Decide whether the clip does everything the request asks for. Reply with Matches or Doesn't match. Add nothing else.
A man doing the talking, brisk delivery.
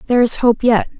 Doesn't match